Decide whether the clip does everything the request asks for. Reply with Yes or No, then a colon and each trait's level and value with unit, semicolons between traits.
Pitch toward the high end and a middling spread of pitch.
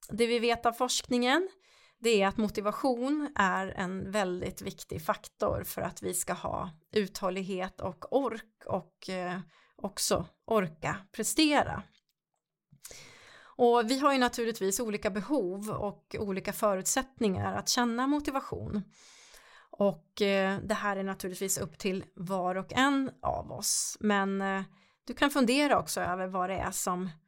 Yes: high, 210 Hz; average, 4.7 semitones